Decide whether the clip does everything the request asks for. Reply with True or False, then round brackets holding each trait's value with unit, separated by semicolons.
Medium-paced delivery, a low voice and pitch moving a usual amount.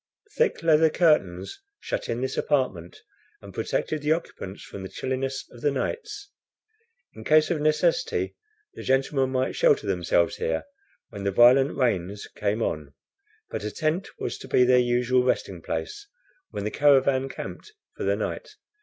True (160 wpm; 130 Hz; 4.9 semitones)